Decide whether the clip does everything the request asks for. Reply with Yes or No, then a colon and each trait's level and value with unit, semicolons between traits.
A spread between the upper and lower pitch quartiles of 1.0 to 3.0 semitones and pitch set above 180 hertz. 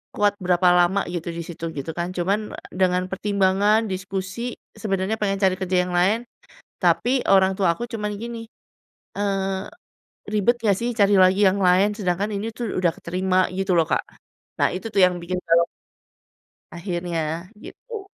Yes: narrow, 2.5 semitones; high, 190 Hz